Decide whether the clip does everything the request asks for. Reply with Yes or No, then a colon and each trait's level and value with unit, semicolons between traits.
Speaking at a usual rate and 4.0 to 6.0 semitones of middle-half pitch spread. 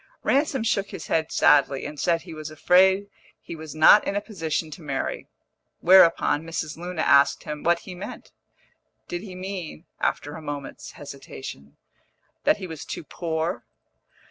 No: average, 160 wpm; average, 3.6 semitones